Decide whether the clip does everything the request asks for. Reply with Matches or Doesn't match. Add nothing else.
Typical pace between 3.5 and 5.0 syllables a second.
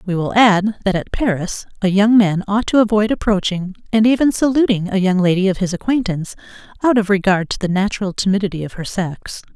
Doesn't match